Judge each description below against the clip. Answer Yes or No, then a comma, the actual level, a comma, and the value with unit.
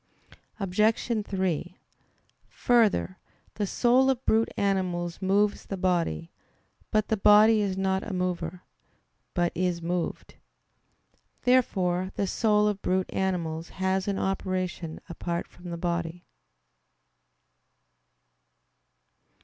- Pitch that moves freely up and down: No, average, 2.9 semitones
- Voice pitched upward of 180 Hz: Yes, high, 190 Hz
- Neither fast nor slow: No, slow, 105 wpm